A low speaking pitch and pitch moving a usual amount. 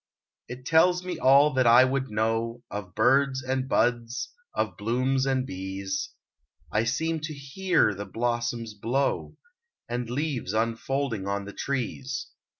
Yes: low, 125 Hz; average, 3.3 semitones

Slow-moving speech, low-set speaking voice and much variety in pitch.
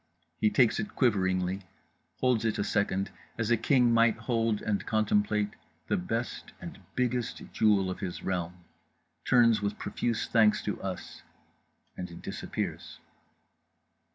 No: slow, 125 wpm; low, 105 Hz; average, 3.1 semitones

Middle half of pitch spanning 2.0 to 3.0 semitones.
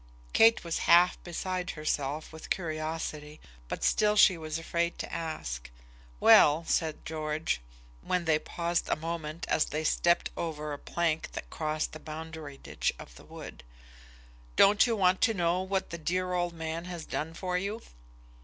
Yes: narrow, 2.6 semitones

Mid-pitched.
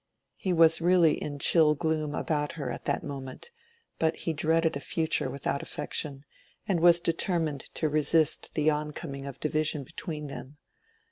Yes: medium, 155 Hz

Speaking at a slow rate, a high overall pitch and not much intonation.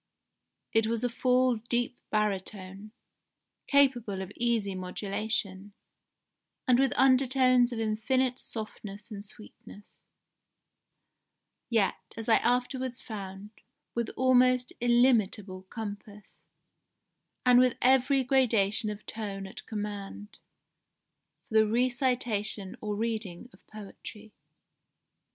No: slow, 100 wpm; high, 225 Hz; average, 3.3 semitones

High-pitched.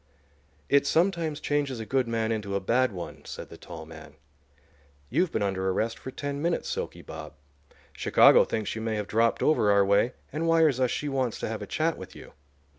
No: low, 115 Hz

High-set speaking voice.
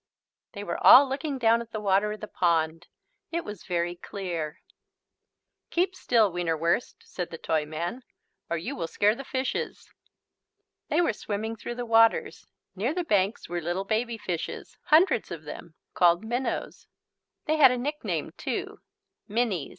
Yes: high, 210 Hz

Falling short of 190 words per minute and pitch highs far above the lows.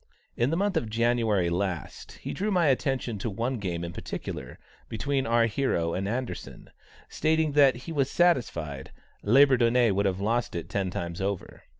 Yes: average, 170 wpm; wide, 5.9 semitones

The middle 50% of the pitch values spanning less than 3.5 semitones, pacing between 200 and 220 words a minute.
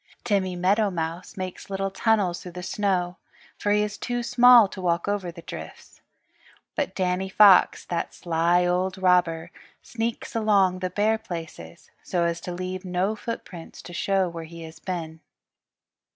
No: average, 2.8 semitones; average, 155 wpm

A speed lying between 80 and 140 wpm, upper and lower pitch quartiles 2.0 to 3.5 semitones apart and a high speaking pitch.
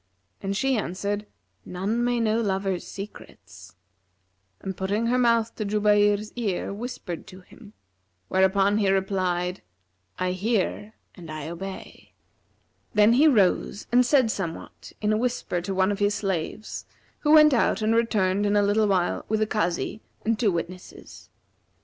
No: average, 155 wpm; average, 2.9 semitones; high, 205 Hz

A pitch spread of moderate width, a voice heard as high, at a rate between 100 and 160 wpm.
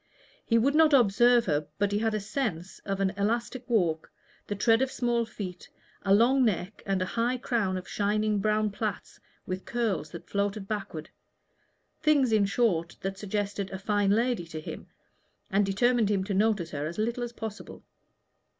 No: average, 3.4 semitones; high, 205 Hz; average, 175 wpm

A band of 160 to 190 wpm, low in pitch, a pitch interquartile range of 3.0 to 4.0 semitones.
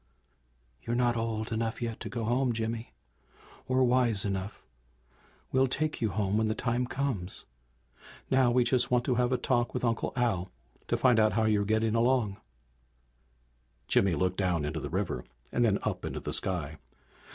Yes: average, 175 wpm; low, 115 Hz; average, 3.5 semitones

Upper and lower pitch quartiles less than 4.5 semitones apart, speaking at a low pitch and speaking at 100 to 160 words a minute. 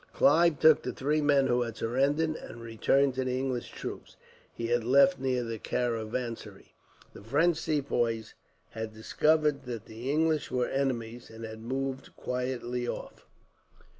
Yes: average, 3.4 semitones; low, 125 Hz; average, 150 wpm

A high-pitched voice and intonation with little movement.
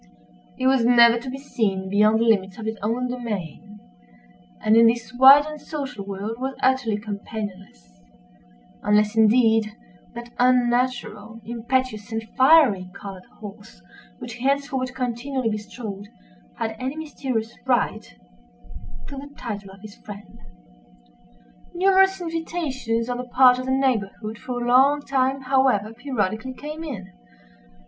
No: high, 235 Hz; average, 3.9 semitones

